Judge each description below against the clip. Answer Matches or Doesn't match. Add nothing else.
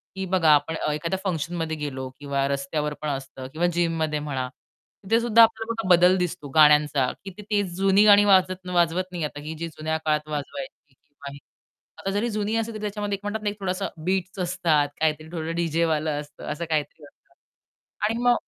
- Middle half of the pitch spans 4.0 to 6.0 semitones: Matches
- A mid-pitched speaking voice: Matches